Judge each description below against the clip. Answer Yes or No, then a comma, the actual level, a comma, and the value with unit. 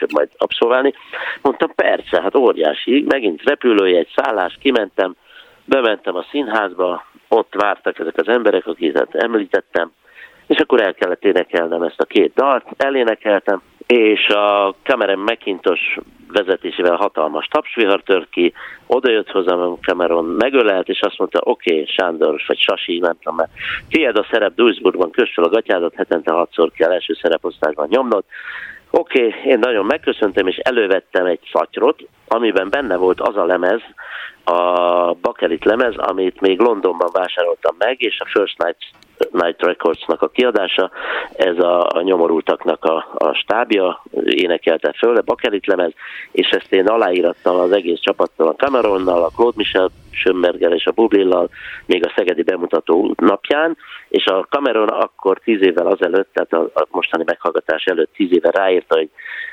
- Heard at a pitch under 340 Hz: No, very high, 400 Hz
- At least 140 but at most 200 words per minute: Yes, average, 150 wpm